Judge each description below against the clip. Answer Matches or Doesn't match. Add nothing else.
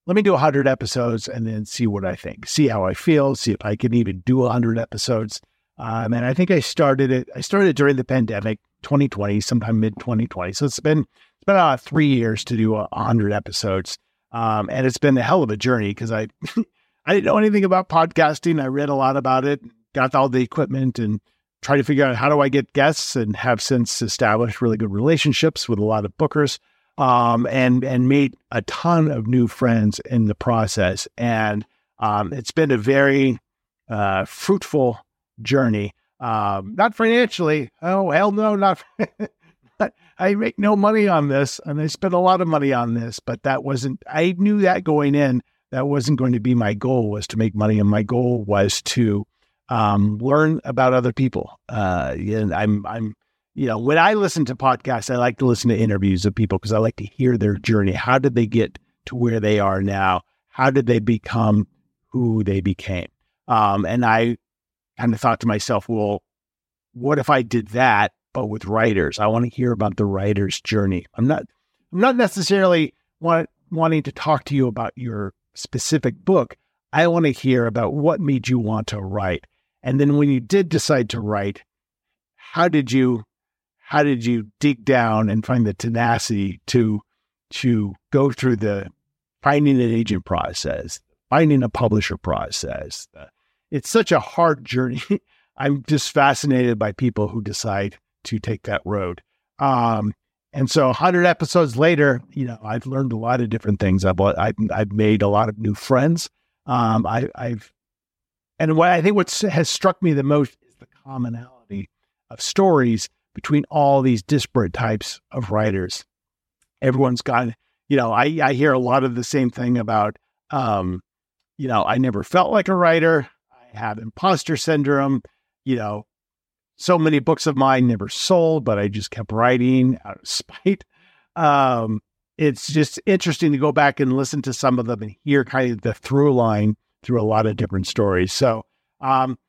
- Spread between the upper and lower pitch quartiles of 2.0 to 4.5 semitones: Doesn't match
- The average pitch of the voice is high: Doesn't match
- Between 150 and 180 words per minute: Doesn't match